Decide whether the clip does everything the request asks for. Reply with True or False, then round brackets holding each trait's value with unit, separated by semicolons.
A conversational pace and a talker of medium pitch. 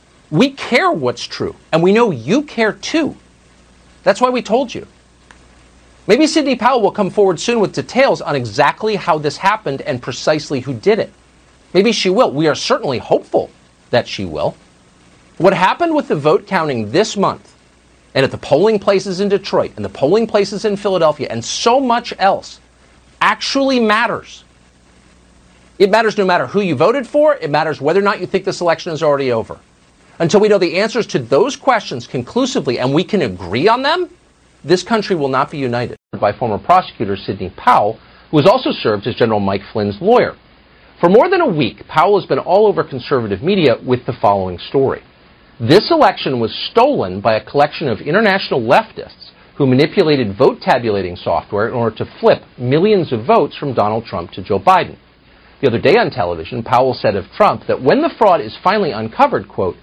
True (190 wpm; 155 Hz)